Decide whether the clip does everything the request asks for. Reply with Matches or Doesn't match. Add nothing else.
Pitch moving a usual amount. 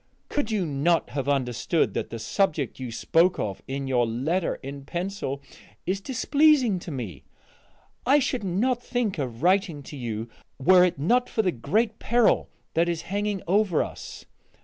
Doesn't match